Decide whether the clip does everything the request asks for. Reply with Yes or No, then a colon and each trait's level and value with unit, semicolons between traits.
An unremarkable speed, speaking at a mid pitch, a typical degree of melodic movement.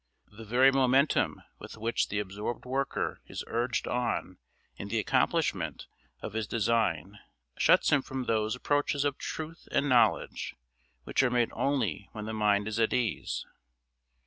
No: average, 150 wpm; low, 115 Hz; average, 3.9 semitones